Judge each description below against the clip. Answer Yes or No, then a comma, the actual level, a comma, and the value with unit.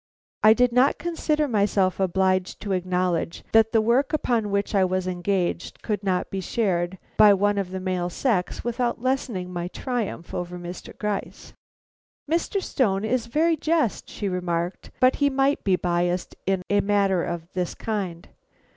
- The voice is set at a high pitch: Yes, high, 200 Hz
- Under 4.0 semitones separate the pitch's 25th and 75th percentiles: No, average, 4.6 semitones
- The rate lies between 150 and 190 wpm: Yes, average, 165 wpm